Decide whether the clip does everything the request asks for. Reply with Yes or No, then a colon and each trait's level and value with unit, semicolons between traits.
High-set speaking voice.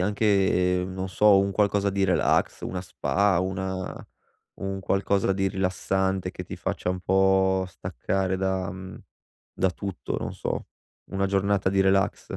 No: very low, 95 Hz